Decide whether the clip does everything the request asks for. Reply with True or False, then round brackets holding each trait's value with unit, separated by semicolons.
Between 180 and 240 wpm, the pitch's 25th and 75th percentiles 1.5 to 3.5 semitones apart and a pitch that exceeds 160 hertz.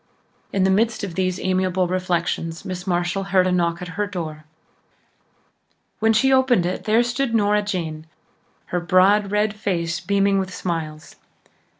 False (155 wpm; 2.9 semitones; 185 Hz)